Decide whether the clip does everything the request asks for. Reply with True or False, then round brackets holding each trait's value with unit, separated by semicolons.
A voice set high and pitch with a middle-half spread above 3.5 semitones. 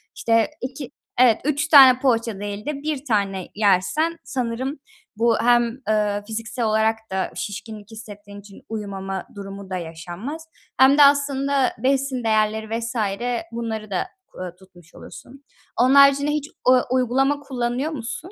True (230 Hz; 4.8 semitones)